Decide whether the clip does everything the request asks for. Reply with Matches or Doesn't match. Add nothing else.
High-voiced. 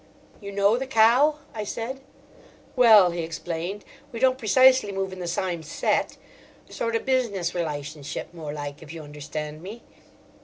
Matches